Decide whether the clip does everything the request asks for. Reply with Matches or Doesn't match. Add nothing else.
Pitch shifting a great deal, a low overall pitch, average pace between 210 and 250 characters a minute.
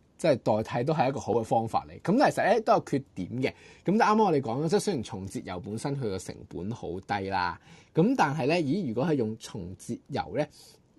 Doesn't match